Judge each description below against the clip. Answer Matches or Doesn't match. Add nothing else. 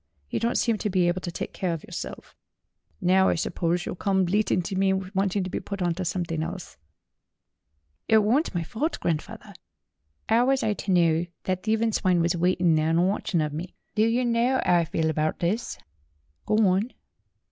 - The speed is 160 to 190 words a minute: Doesn't match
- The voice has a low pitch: Doesn't match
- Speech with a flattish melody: Doesn't match